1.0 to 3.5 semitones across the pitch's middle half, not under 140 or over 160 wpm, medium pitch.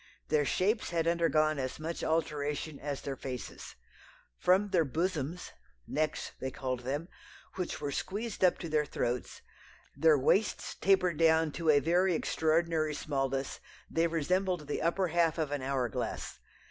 Yes: average, 3.2 semitones; average, 150 wpm; medium, 155 Hz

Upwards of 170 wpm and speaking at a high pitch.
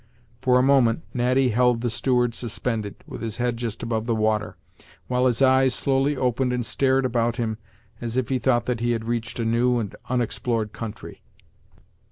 No: average, 185 wpm; low, 120 Hz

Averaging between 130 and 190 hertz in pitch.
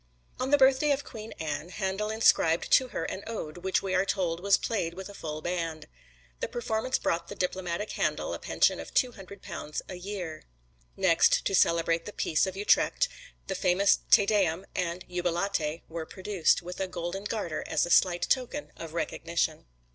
Yes: medium, 185 Hz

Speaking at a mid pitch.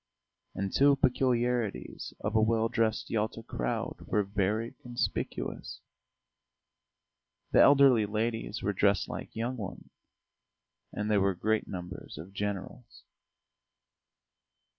No: low, 110 Hz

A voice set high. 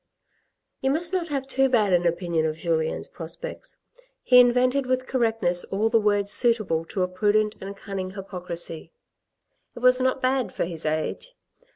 Yes: high, 210 Hz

